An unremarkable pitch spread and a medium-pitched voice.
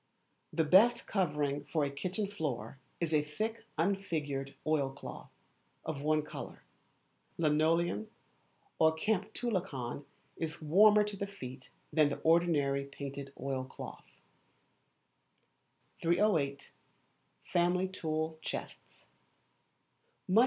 Yes: average, 4.7 semitones; medium, 155 Hz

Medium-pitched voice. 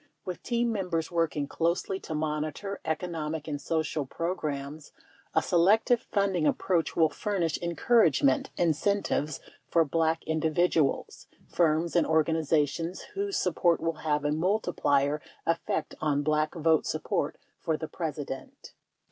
Yes: medium, 160 Hz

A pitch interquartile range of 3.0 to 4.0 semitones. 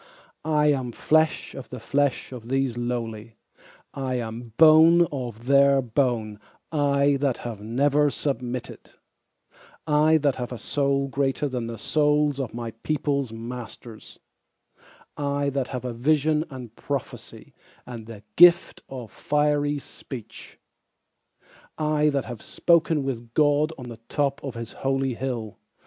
Yes: average, 3.5 semitones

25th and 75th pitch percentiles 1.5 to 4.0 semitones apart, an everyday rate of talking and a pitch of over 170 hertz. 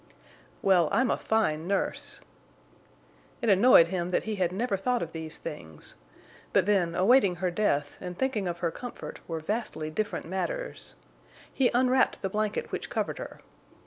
No: average, 4.6 semitones; average, 160 wpm; high, 190 Hz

